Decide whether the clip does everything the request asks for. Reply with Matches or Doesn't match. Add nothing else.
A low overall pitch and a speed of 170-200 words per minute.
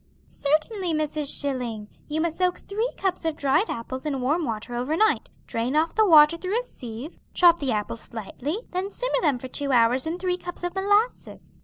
Doesn't match